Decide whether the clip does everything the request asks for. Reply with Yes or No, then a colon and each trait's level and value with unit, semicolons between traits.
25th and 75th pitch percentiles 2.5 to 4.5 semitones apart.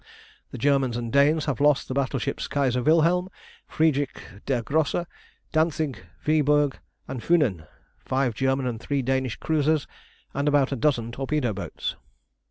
Yes: average, 2.8 semitones